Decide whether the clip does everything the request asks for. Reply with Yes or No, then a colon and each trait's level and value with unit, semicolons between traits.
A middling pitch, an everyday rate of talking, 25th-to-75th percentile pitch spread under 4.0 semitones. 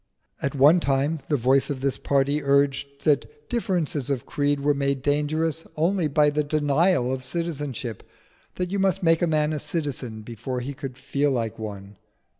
Yes: medium, 145 Hz; average, 175 wpm; average, 2.7 semitones